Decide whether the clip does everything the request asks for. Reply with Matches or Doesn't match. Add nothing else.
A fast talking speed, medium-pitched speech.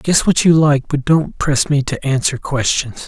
Matches